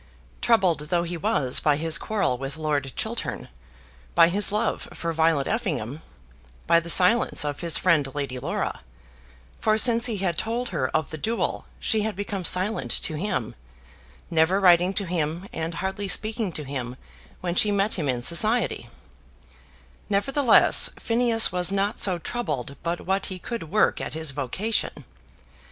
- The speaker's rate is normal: Yes, average, 160 wpm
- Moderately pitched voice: Yes, medium, 180 Hz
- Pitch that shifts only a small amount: No, average, 5.1 semitones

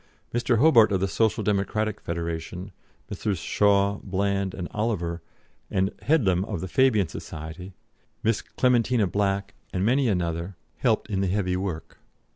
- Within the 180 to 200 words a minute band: No, average, 140 wpm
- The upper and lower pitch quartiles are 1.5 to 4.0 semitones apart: Yes, average, 3.0 semitones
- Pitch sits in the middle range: No, low, 100 Hz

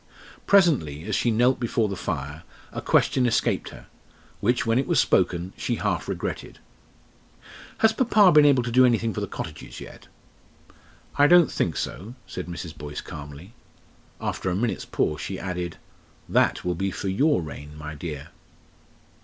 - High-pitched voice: No, low, 100 Hz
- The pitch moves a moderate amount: No, wide, 7.5 semitones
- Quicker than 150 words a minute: Yes, average, 160 wpm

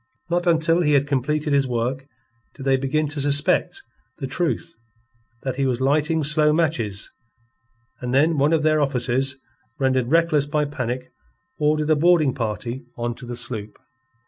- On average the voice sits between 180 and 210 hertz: No, medium, 140 Hz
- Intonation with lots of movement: No, average, 3.1 semitones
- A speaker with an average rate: Yes, average, 160 wpm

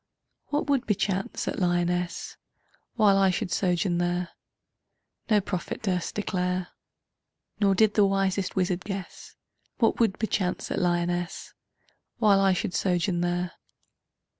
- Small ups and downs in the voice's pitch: Yes, narrow, 2.2 semitones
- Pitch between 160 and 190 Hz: Yes, medium, 185 Hz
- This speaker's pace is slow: Yes, slow, 125 wpm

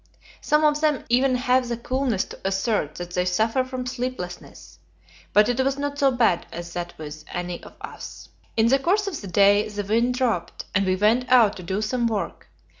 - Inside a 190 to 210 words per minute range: Yes, average, 200 wpm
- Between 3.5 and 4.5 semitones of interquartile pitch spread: No, wide, 5.5 semitones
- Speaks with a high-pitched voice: Yes, high, 230 Hz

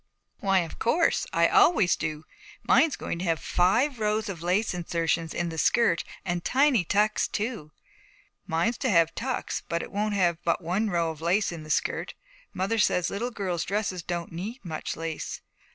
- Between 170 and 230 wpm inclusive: Yes, average, 180 wpm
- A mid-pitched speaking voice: Yes, medium, 180 Hz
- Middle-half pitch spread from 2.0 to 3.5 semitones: No, average, 4.3 semitones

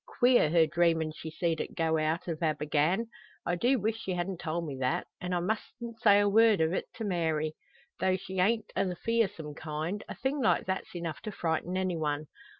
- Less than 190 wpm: No, average, 195 wpm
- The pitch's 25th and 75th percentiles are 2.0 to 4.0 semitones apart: No, average, 4.4 semitones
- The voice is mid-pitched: Yes, medium, 175 Hz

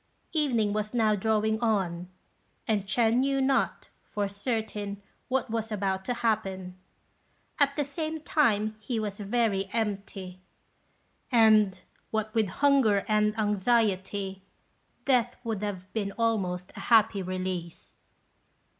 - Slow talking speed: Yes, slow, 120 wpm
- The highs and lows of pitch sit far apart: No, average, 2.8 semitones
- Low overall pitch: No, high, 215 Hz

